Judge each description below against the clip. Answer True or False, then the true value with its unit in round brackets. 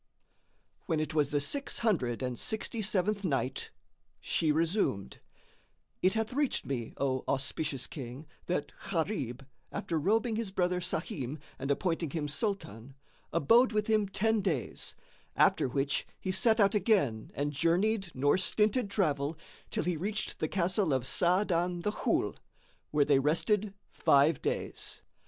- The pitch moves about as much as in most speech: False (6.7 semitones)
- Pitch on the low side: False (170 Hz)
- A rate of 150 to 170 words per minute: False (140 wpm)